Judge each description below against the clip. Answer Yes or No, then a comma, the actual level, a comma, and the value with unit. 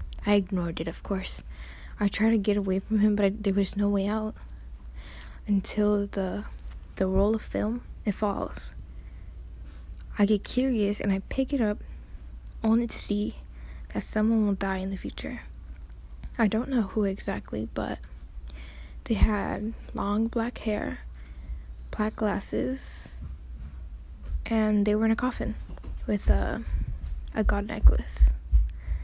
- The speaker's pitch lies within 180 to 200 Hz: Yes, high, 190 Hz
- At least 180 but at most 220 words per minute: No, average, 145 wpm